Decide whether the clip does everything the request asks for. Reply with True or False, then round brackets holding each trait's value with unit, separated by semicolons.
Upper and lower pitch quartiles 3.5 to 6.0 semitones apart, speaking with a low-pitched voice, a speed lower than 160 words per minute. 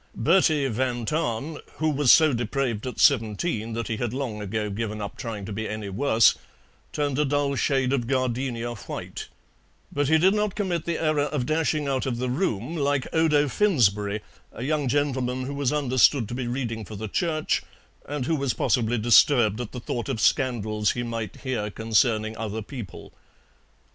False (4.4 semitones; 125 Hz; 180 wpm)